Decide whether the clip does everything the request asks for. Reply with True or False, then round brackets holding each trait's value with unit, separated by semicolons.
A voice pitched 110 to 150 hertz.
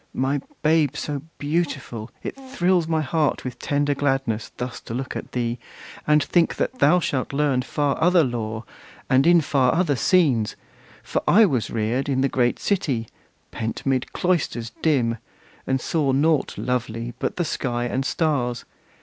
True (135 Hz)